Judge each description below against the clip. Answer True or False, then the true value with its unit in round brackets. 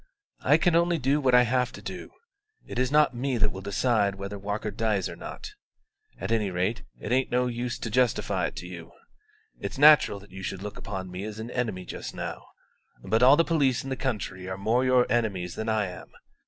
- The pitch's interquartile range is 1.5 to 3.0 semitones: False (4.4 semitones)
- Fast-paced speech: True (220 wpm)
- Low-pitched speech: True (115 Hz)